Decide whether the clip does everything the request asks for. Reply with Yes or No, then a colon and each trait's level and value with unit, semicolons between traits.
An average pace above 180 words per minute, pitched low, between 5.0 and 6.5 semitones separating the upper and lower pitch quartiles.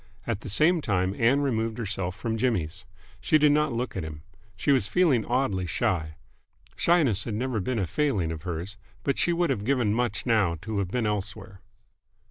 Yes: average, 190 wpm; low, 110 Hz; wide, 5.4 semitones